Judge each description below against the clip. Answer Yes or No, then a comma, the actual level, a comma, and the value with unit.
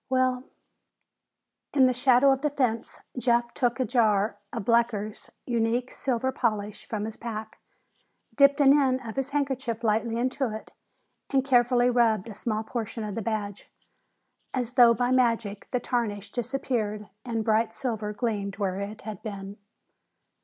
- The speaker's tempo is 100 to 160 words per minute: Yes, average, 155 wpm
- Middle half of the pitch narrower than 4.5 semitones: Yes, average, 3.0 semitones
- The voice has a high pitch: Yes, high, 235 Hz